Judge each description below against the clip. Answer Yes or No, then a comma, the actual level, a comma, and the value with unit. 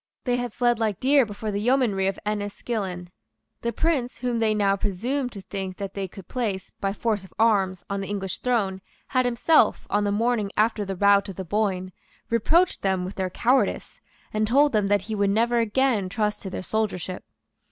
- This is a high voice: Yes, high, 210 Hz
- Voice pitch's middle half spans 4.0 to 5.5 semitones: No, average, 3.4 semitones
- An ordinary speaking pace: Yes, average, 195 wpm